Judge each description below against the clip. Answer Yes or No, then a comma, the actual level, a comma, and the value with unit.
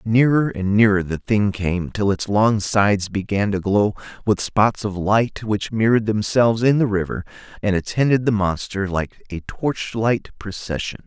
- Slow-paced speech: No, average, 170 wpm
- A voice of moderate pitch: No, low, 105 Hz